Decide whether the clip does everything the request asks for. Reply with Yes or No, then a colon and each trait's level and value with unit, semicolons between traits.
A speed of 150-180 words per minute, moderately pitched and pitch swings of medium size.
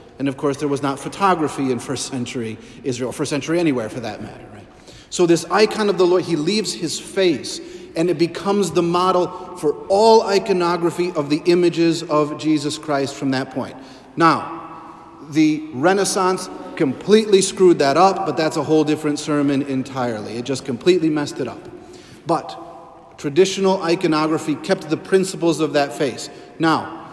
Yes: average, 170 wpm; medium, 160 Hz; average, 3.9 semitones